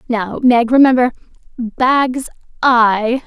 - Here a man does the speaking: No, female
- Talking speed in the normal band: No, slow, 75 wpm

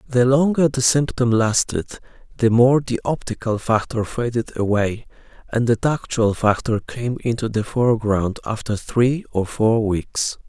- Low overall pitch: Yes, low, 120 Hz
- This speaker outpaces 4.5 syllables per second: No, 4.3 syllables/s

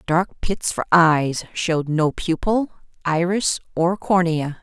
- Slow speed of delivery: Yes, slow, 130 wpm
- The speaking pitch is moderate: Yes, medium, 170 Hz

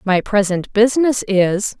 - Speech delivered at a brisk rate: No, slow, 135 wpm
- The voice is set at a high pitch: Yes, high, 210 Hz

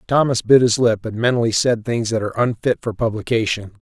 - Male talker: Yes, male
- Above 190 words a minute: Yes, fast, 205 wpm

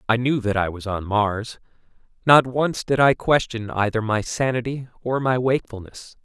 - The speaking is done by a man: Yes, male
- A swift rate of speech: No, average, 175 wpm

